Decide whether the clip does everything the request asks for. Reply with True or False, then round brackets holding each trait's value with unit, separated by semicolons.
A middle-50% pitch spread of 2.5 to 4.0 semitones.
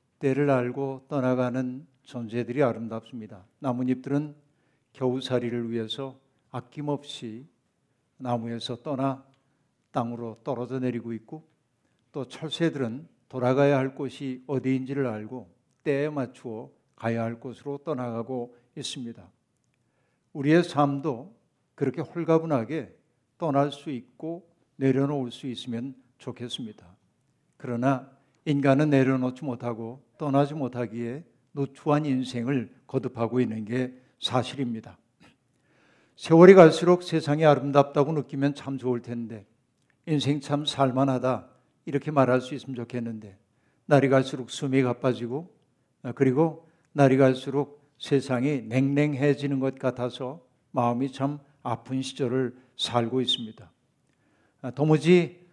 True (2.8 semitones)